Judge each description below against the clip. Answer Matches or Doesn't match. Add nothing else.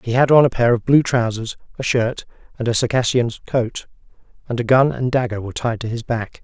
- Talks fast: Matches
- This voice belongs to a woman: Doesn't match